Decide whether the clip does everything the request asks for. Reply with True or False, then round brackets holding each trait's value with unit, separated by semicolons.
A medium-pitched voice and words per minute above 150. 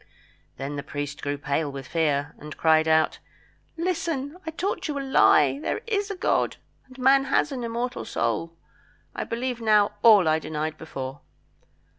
True (165 Hz; 165 wpm)